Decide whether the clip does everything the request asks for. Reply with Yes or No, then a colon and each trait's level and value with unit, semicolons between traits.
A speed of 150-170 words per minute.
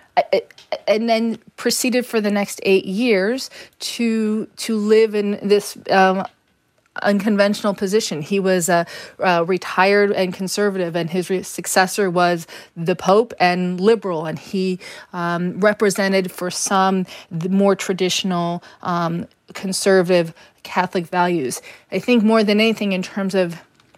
No: average, 140 wpm